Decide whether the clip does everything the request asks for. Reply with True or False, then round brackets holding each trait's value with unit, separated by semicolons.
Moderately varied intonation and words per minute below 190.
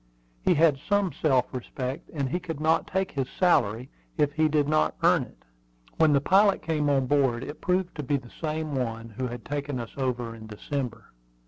False (3.8 semitones; 200 wpm)